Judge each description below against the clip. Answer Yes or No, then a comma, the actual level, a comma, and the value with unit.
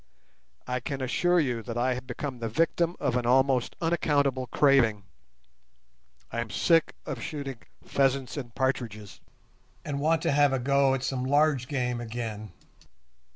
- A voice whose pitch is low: Yes, low, 130 Hz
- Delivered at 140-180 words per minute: Yes, average, 150 wpm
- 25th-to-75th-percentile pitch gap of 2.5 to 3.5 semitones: Yes, average, 2.8 semitones